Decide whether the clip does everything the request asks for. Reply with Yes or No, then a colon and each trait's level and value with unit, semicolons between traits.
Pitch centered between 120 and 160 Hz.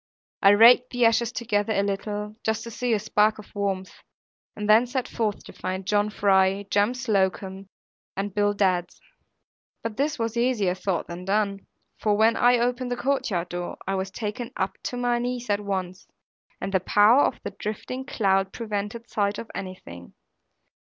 No: high, 210 Hz